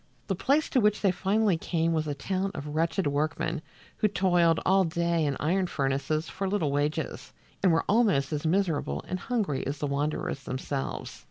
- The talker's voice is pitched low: No, medium, 165 Hz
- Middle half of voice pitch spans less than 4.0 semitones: No, average, 4.6 semitones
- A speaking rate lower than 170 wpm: No, average, 180 wpm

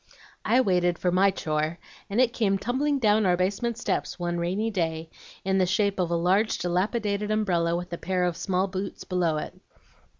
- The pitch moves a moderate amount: Yes, average, 3.2 semitones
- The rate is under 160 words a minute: No, average, 190 wpm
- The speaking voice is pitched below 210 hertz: Yes, medium, 185 Hz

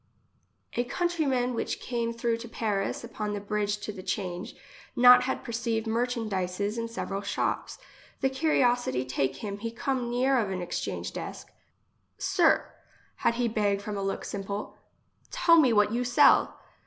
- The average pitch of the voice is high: Yes, high, 230 Hz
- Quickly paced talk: No, average, 165 wpm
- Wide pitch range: No, average, 3.4 semitones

